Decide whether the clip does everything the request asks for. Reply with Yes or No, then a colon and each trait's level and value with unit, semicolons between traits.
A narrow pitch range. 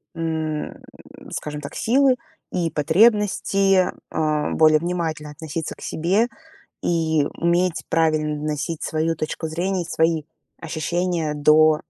Yes: narrow, 2.3 semitones